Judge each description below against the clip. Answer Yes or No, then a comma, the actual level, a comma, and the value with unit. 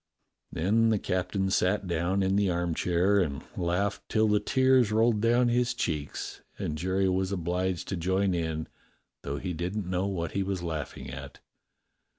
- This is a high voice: No, very low, 95 Hz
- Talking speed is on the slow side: No, average, 160 wpm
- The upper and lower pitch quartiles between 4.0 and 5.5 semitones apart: No, average, 3.0 semitones